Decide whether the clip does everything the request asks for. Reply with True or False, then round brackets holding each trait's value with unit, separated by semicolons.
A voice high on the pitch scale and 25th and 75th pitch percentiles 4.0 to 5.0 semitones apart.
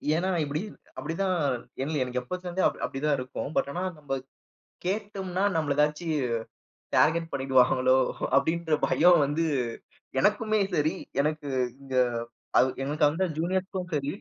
False (155 Hz; 4.3 semitones)